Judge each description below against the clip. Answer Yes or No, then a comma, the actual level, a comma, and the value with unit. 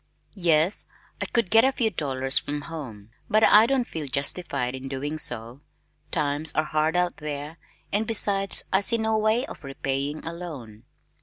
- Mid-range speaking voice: Yes, medium, 155 Hz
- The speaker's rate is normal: Yes, average, 170 wpm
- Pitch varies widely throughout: Yes, wide, 6.7 semitones